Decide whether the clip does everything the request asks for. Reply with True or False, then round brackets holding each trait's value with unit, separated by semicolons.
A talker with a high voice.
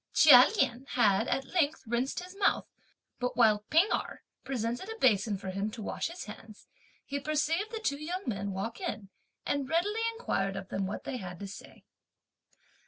True (250 Hz)